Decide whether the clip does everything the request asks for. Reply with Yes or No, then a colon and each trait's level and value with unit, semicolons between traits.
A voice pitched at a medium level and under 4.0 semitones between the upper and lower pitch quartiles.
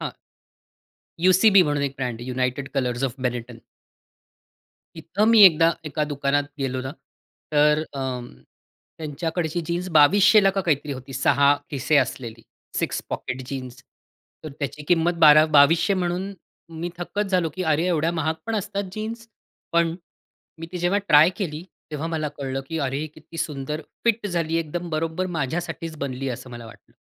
No: medium, 155 Hz; average, 4.3 semitones